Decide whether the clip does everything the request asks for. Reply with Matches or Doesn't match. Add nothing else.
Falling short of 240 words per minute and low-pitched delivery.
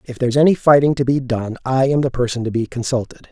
Doesn't match